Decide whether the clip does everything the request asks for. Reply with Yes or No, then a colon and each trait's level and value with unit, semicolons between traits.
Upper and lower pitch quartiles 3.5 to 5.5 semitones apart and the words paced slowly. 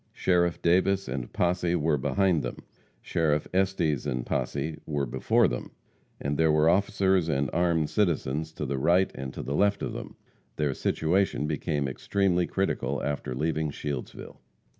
No: average, 3.9 semitones; average, 155 wpm